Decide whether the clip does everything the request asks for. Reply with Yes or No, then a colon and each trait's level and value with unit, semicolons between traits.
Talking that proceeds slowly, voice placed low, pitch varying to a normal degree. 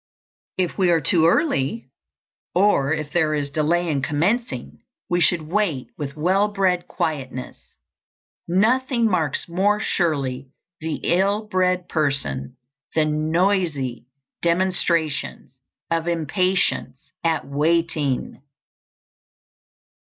No: slow, 100 wpm; medium, 165 Hz; average, 4.1 semitones